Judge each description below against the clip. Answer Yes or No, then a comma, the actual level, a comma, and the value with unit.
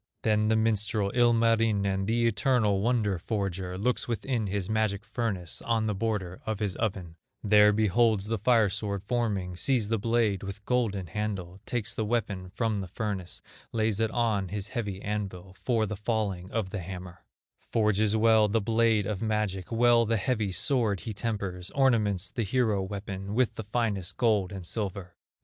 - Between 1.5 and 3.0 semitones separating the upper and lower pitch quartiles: Yes, narrow, 2.6 semitones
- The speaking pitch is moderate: No, low, 105 Hz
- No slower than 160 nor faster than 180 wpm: Yes, average, 165 wpm